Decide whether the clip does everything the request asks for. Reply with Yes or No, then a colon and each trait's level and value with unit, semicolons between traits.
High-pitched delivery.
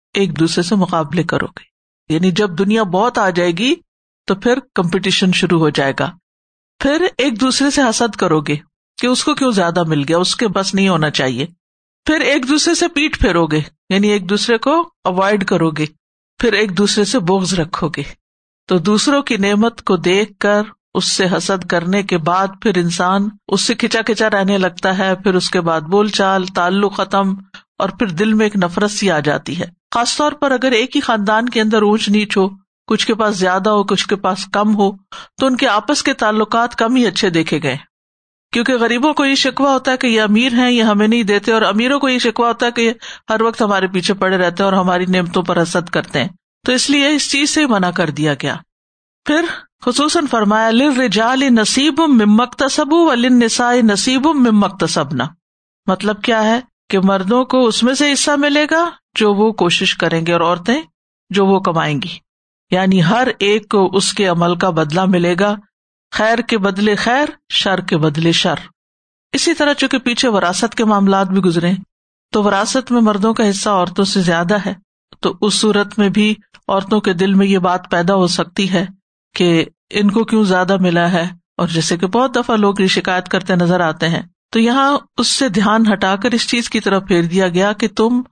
Yes: high, 205 Hz